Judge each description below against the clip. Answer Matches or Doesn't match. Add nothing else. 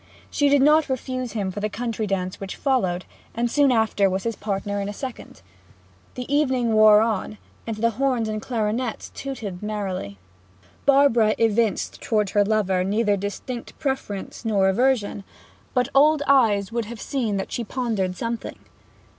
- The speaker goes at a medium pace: Matches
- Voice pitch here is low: Doesn't match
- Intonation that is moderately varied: Matches